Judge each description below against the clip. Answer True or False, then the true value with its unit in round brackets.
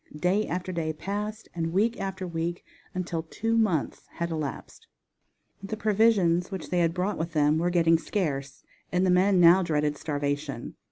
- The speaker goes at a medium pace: True (165 wpm)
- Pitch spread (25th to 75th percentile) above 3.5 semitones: False (3.2 semitones)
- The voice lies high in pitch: False (175 Hz)